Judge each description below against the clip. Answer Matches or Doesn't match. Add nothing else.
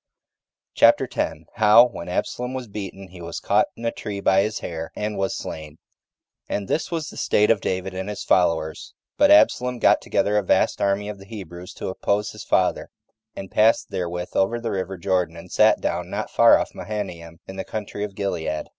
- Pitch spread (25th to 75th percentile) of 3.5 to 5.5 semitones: Doesn't match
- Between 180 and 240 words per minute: Matches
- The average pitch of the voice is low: Matches